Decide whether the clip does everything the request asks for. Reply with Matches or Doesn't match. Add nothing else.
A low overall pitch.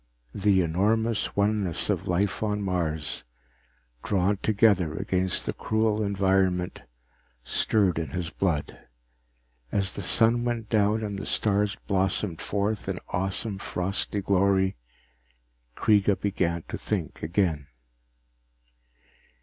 Matches